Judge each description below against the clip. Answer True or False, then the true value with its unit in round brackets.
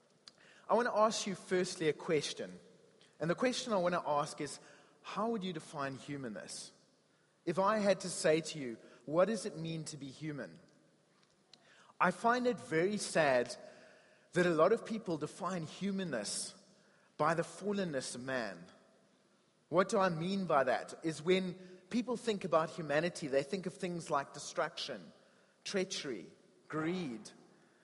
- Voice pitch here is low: False (180 Hz)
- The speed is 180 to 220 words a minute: False (155 wpm)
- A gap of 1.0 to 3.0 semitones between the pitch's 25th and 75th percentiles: False (4.2 semitones)